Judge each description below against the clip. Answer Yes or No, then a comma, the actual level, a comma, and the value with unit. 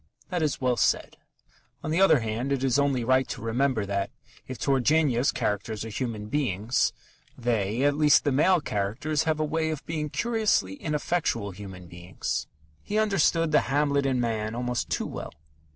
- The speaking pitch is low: Yes, low, 130 Hz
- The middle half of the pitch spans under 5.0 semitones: No, wide, 5.6 semitones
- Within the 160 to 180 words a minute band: Yes, average, 170 wpm